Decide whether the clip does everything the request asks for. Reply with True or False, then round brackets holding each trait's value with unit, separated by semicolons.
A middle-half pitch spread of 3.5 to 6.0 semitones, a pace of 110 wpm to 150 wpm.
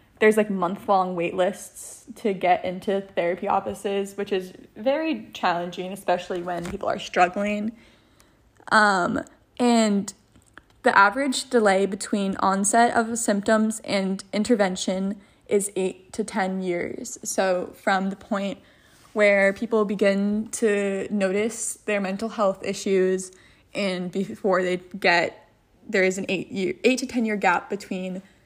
False (2.4 semitones; 135 wpm)